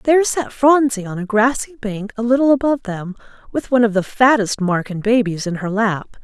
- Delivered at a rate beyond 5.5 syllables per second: No, 5.4 syllables/s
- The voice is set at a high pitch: Yes, high, 225 Hz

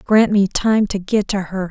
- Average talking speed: No, fast, 245 wpm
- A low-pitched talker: No, high, 200 Hz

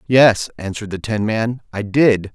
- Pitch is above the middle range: No, low, 110 Hz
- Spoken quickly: No, average, 180 wpm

